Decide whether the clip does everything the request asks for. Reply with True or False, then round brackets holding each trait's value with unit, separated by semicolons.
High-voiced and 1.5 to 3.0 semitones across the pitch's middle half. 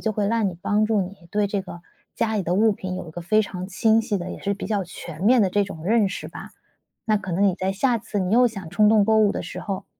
True (200 Hz; 2.6 semitones)